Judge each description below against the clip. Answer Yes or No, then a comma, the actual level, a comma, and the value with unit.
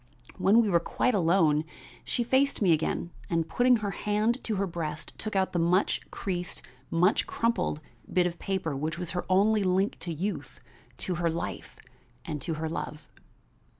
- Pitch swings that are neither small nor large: Yes, average, 3.9 semitones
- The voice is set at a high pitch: No, medium, 180 Hz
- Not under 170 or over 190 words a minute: Yes, average, 175 wpm